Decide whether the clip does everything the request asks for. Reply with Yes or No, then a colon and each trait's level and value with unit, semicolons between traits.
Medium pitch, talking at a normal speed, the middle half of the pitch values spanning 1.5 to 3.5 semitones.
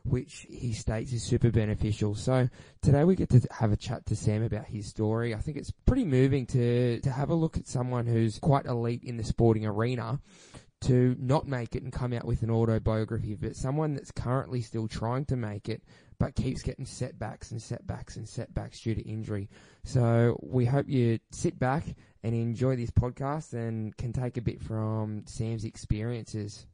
No: low, 120 Hz; average, 195 wpm; narrow, 2.5 semitones